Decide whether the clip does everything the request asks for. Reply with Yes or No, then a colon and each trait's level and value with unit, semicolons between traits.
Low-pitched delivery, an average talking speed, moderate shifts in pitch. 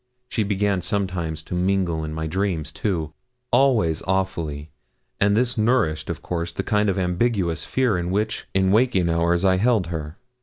Yes: very low, 95 Hz; average, 165 wpm; average, 3.8 semitones